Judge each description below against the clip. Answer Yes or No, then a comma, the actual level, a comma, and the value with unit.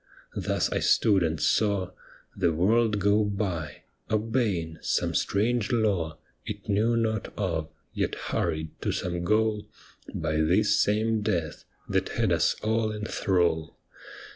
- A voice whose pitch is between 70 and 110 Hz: Yes, low, 100 Hz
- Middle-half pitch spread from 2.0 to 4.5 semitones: Yes, average, 4.0 semitones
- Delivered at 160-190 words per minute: No, slow, 135 wpm